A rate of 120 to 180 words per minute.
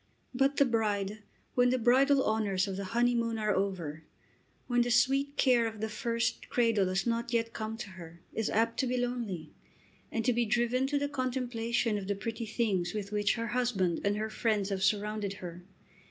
No: average, 195 wpm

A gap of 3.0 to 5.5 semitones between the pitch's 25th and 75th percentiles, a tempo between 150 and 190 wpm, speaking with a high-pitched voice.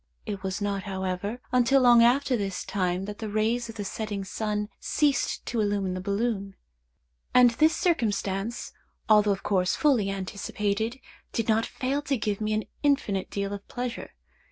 Yes: average, 3.4 semitones; average, 165 wpm; high, 210 Hz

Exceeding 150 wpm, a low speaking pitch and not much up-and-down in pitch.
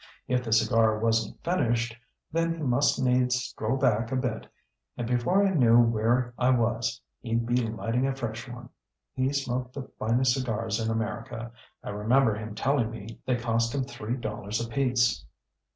Yes: average, 170 wpm; low, 120 Hz; narrow, 2.1 semitones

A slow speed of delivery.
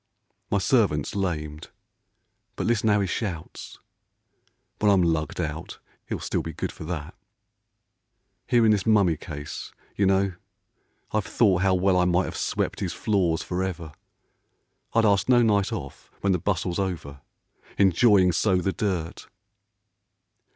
No: average, 150 wpm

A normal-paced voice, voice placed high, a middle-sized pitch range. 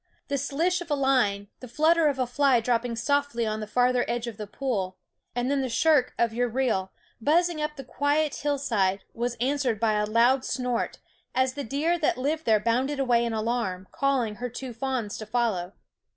Yes: average, 195 wpm; very high, 250 Hz; average, 3.7 semitones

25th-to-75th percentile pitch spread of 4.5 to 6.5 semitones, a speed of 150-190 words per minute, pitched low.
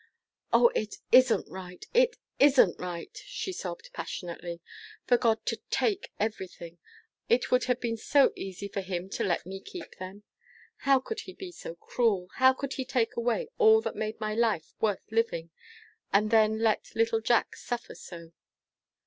No: wide, 5.5 semitones; average, 165 wpm; high, 225 Hz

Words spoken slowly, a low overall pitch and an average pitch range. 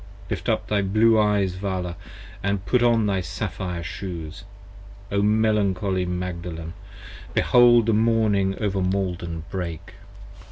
Yes: slow, 120 wpm; very low, 95 Hz; average, 3.0 semitones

